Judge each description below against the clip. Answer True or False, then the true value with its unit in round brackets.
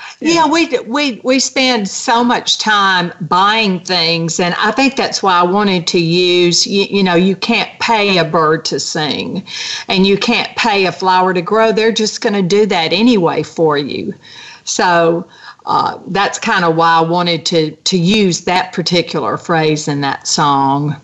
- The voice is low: False (185 Hz)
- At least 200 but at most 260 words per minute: False (175 wpm)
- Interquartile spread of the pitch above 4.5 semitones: True (4.9 semitones)